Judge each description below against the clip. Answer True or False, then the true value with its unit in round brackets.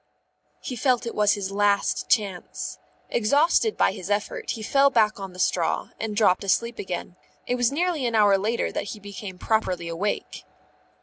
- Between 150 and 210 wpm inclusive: True (180 wpm)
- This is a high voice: True (210 Hz)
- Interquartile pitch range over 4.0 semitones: False (3.3 semitones)